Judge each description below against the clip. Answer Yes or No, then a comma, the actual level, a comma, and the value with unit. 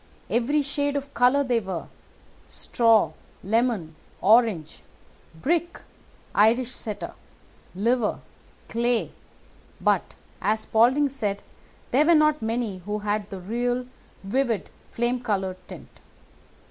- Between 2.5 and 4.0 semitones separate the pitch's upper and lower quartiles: Yes, average, 3.7 semitones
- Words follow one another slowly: Yes, slow, 105 wpm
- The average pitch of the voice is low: No, high, 235 Hz